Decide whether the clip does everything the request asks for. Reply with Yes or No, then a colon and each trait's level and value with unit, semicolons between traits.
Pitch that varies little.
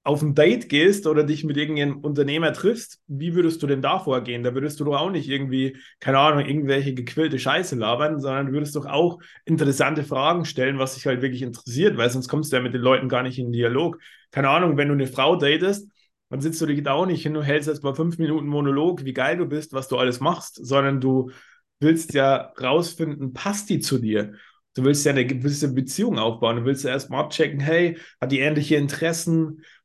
No: average, 3.1 semitones